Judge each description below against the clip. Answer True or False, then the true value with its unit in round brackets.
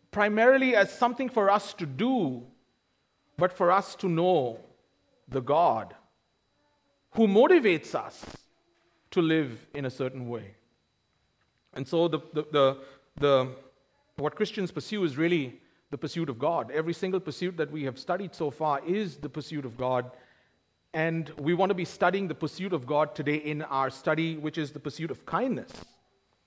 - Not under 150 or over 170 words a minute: True (165 wpm)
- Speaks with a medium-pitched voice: True (160 Hz)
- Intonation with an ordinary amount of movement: True (4.6 semitones)